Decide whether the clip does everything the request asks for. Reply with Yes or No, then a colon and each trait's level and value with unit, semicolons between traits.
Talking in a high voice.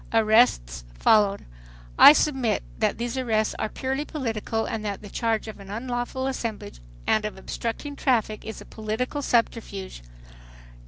Yes: high, 225 Hz